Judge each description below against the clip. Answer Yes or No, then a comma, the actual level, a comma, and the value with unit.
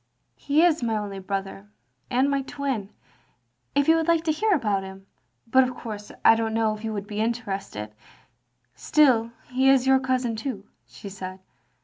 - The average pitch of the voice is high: Yes, high, 225 Hz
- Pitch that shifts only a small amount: No, average, 5.3 semitones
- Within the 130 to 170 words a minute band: No, average, 195 wpm